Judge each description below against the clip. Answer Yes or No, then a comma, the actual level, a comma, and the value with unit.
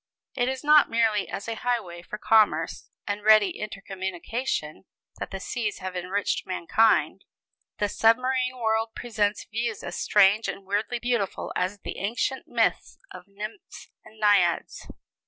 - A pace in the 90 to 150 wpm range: Yes, average, 140 wpm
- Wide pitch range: No, average, 3.0 semitones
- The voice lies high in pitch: Yes, high, 210 Hz